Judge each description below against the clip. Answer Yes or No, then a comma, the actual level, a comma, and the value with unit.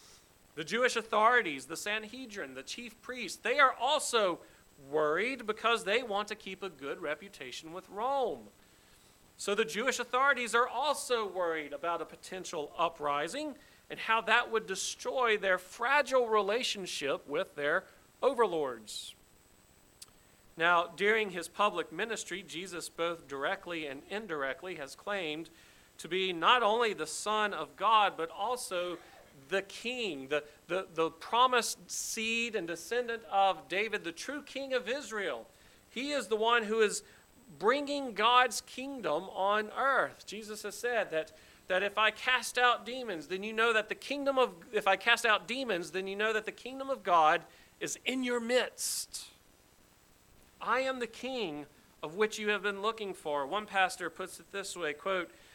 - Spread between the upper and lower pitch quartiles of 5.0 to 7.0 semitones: Yes, wide, 5.6 semitones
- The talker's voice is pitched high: Yes, high, 205 Hz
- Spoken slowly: No, average, 155 wpm